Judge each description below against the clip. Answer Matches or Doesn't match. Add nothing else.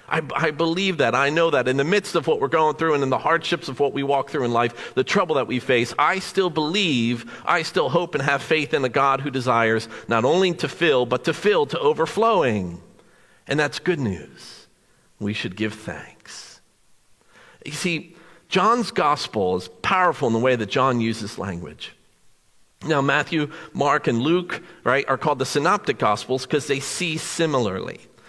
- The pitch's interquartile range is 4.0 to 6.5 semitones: Matches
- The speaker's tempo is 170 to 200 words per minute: Matches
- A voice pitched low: Doesn't match